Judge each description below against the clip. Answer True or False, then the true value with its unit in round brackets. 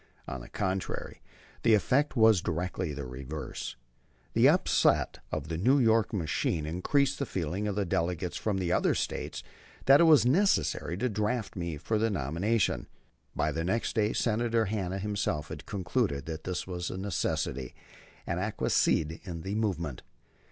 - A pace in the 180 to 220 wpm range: False (150 wpm)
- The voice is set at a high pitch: False (95 Hz)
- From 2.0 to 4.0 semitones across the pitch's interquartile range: False (5.2 semitones)